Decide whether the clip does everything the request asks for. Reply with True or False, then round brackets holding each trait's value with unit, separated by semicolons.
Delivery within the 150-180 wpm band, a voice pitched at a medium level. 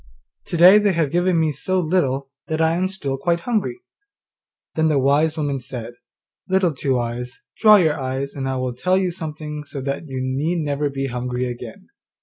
False (190 wpm; 150 Hz)